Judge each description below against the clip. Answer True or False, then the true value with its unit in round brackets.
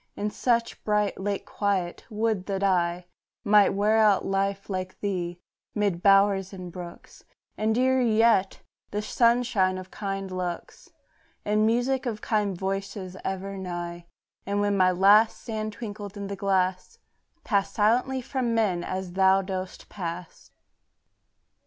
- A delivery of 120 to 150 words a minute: True (140 wpm)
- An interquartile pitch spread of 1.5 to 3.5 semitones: True (2.5 semitones)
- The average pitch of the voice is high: True (200 Hz)